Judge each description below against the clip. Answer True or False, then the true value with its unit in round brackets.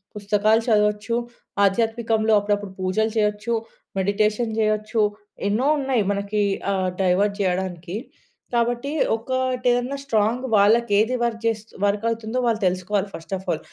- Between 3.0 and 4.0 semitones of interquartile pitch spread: False (2.5 semitones)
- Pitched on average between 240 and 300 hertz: False (215 Hz)